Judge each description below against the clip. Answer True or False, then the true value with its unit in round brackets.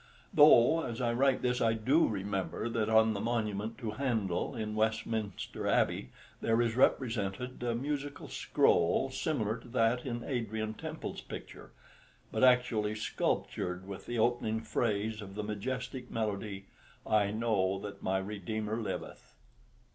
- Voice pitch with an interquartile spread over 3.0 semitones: False (2.7 semitones)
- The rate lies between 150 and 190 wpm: False (140 wpm)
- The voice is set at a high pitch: False (110 Hz)